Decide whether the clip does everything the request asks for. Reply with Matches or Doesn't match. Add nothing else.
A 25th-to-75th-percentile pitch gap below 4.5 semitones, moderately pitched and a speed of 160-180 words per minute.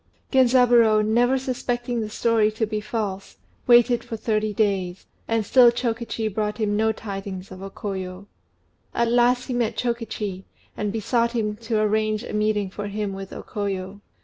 Doesn't match